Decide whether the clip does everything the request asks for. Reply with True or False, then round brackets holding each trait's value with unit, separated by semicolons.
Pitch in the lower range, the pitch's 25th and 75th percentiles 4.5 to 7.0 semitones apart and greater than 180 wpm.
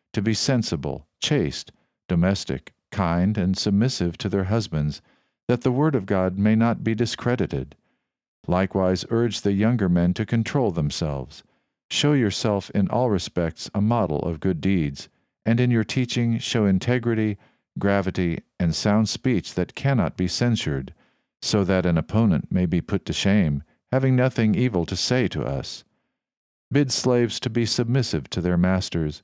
False (100 Hz; 4.8 semitones; 155 wpm)